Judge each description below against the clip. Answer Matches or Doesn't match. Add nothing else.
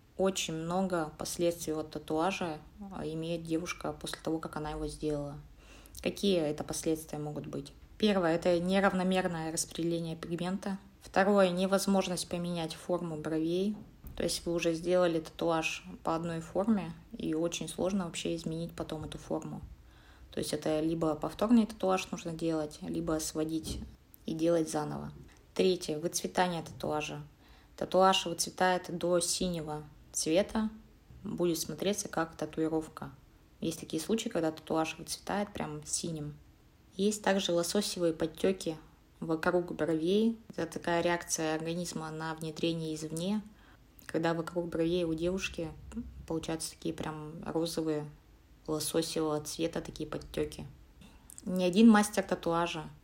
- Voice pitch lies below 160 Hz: Doesn't match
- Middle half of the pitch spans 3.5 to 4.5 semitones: Doesn't match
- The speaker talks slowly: Doesn't match